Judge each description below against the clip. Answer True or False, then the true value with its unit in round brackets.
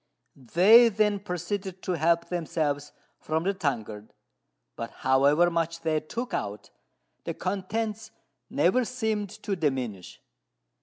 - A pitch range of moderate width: False (5.8 semitones)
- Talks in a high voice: False (175 Hz)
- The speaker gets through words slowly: True (115 wpm)